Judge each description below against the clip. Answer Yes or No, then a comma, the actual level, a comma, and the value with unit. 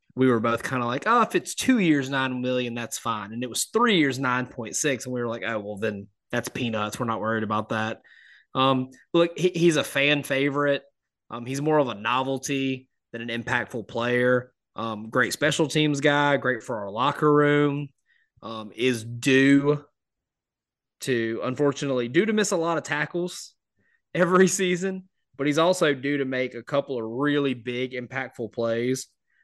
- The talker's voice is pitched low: Yes, low, 130 Hz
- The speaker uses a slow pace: No, average, 180 wpm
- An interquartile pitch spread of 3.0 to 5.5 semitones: Yes, average, 3.4 semitones